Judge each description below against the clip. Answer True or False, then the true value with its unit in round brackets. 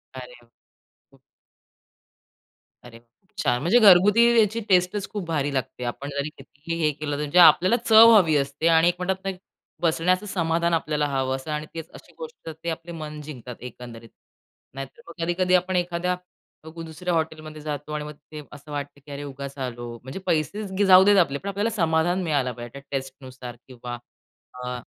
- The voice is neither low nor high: True (155 Hz)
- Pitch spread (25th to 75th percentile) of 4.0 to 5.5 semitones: True (4.5 semitones)